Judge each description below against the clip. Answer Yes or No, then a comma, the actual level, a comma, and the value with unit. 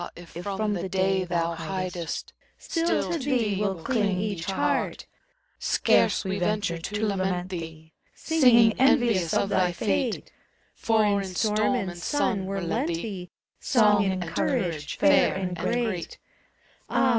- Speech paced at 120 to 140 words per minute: Yes, slow, 135 wpm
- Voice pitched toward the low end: No, high, 190 Hz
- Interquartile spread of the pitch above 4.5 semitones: No, average, 3.6 semitones